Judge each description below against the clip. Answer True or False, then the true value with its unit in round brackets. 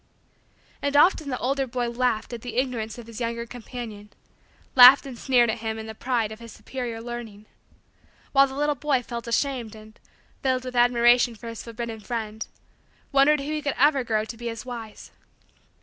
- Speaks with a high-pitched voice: True (240 Hz)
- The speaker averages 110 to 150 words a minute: False (180 wpm)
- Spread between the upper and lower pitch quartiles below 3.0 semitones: True (2.5 semitones)